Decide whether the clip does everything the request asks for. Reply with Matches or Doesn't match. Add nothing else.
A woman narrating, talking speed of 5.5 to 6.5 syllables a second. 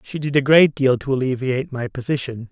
Doesn't match